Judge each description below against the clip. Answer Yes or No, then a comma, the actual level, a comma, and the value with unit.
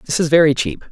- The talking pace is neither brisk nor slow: No, fast, 265 wpm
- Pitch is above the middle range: No, medium, 145 Hz